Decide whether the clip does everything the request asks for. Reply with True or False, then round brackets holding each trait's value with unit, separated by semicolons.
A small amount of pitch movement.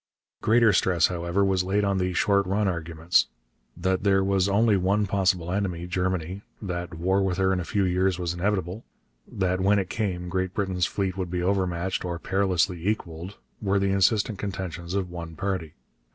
True (1.9 semitones)